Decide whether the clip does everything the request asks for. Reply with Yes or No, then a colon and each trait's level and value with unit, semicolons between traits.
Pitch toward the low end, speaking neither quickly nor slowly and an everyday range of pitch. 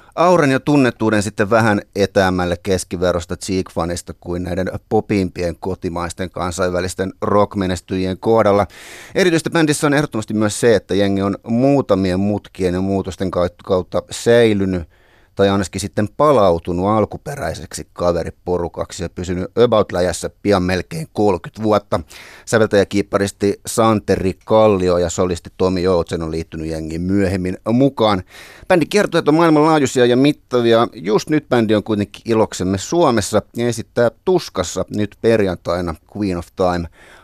Yes: low, 100 Hz; average, 125 wpm; average, 3.8 semitones